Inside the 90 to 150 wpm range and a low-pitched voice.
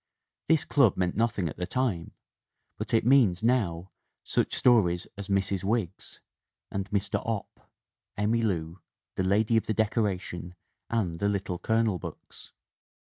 Yes: average, 140 wpm; low, 100 Hz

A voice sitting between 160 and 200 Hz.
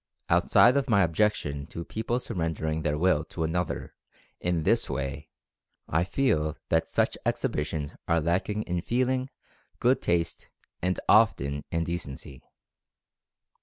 No: very low, 85 Hz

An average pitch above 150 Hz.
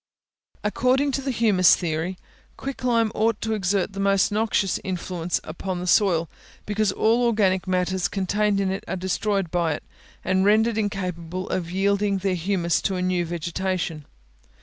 Yes: high, 190 Hz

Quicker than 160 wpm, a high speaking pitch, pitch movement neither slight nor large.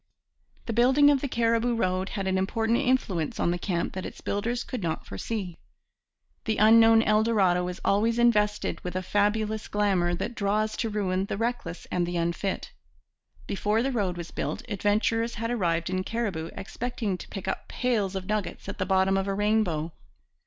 Yes: average, 180 wpm; high, 205 Hz; average, 3.6 semitones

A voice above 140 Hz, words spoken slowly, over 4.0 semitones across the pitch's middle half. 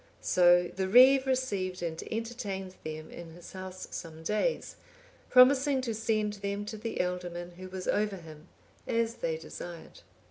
No: high, 190 Hz; average, 150 wpm; average, 4.6 semitones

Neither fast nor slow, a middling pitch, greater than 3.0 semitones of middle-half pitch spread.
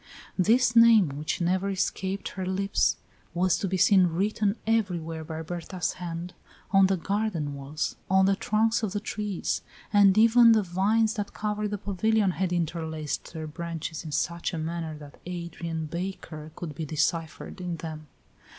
Yes: average, 160 wpm; medium, 180 Hz; average, 3.9 semitones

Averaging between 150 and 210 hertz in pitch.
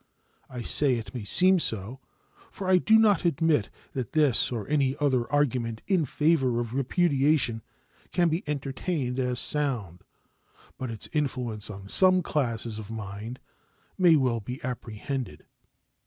No: low, 130 Hz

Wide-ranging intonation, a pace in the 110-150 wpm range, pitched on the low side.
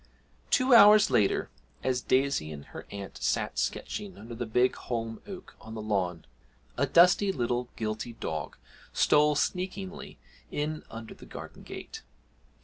Yes: wide, 8.5 semitones; average, 140 wpm; low, 125 Hz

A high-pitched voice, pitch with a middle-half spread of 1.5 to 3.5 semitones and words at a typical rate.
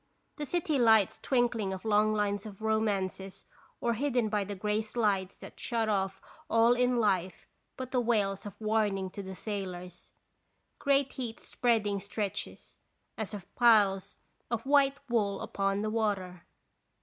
Yes: high, 215 Hz; average, 3.1 semitones; average, 150 wpm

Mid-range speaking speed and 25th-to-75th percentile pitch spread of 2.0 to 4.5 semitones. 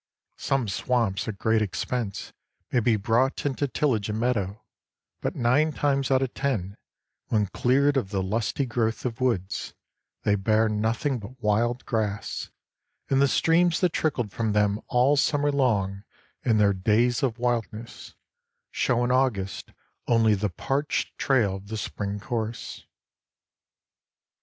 Yes: average, 145 wpm; average, 3.9 semitones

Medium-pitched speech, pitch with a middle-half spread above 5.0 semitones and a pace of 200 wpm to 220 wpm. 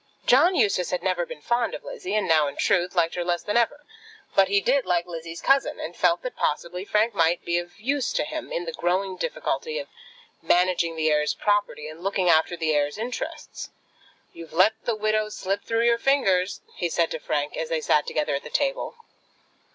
Yes: medium, 180 Hz; wide, 5.4 semitones; fast, 205 wpm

